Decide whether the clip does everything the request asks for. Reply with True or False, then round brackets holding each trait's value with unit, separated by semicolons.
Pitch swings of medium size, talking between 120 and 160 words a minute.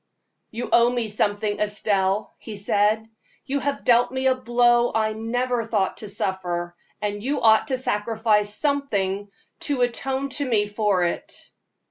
True (3.1 semitones; 150 wpm)